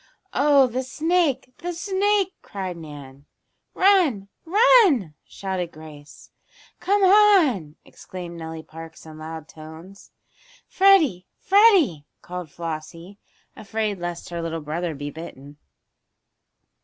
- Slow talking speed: Yes, slow, 105 wpm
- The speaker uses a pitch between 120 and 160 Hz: No, medium, 185 Hz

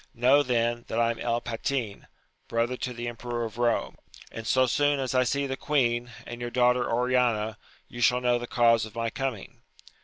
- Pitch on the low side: Yes, low, 120 Hz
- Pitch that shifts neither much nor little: No, narrow, 1.4 semitones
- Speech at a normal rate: Yes, average, 195 wpm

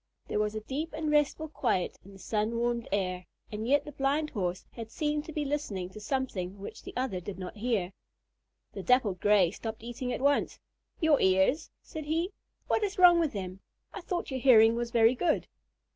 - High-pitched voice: Yes, high, 240 Hz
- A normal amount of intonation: No, wide, 6.5 semitones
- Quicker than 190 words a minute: Yes, average, 200 wpm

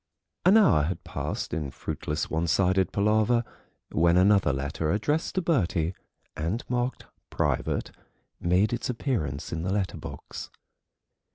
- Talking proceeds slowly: Yes, slow, 130 wpm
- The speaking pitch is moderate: No, very low, 95 Hz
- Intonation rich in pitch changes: Yes, wide, 6.6 semitones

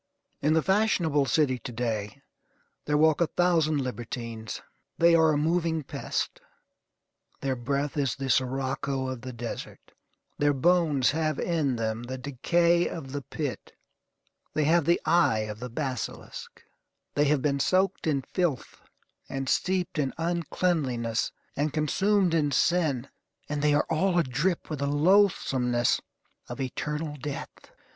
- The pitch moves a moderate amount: Yes, average, 4.2 semitones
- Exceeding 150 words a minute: No, average, 140 wpm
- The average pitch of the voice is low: No, medium, 145 Hz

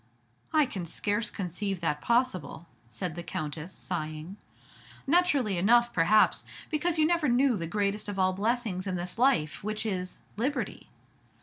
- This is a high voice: Yes, high, 205 Hz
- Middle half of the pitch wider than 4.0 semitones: Yes, wide, 5.5 semitones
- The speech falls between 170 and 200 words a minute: No, average, 145 wpm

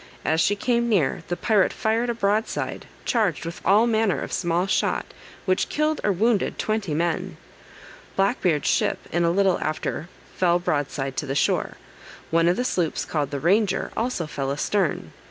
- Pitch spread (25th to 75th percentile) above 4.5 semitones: Yes, average, 5.1 semitones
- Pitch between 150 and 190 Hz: Yes, medium, 185 Hz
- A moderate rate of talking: Yes, average, 175 wpm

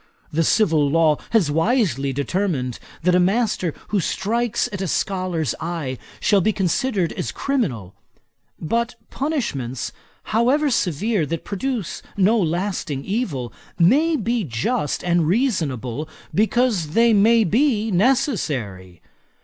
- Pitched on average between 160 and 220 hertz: Yes, medium, 185 Hz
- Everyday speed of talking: No, slow, 120 wpm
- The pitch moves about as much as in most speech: No, wide, 7.2 semitones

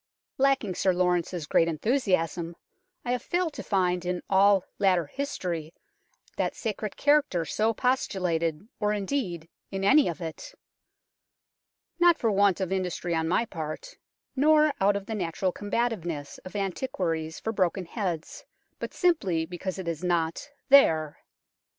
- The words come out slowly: No, average, 145 wpm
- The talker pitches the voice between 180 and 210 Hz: Yes, high, 190 Hz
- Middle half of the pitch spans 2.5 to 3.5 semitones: No, average, 5.1 semitones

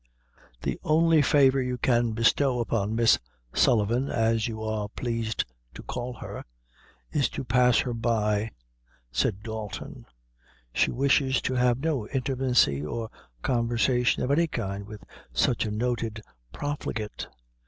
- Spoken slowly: Yes, slow, 130 wpm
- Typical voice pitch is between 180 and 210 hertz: No, low, 120 Hz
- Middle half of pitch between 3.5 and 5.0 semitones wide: No, average, 3.0 semitones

